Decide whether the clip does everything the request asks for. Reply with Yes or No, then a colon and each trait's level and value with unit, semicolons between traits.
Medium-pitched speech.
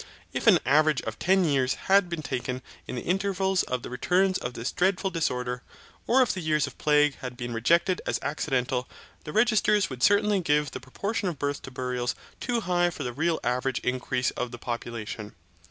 Yes: medium, 150 Hz